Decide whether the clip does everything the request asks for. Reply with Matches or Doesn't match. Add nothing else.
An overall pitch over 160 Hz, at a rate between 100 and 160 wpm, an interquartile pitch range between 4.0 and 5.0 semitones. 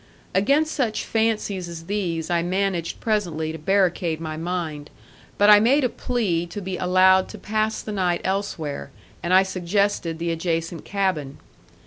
Doesn't match